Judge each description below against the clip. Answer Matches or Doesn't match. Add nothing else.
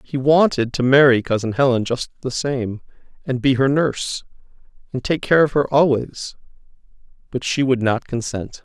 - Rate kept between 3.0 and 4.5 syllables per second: Doesn't match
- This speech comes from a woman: Doesn't match